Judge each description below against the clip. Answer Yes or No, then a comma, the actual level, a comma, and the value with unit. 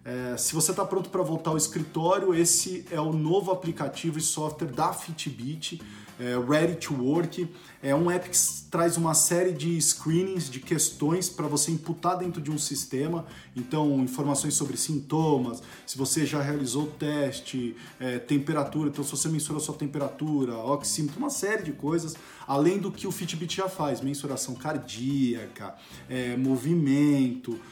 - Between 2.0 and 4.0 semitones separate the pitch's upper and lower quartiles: Yes, average, 3.5 semitones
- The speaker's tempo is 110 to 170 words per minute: Yes, average, 160 wpm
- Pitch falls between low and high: Yes, medium, 150 Hz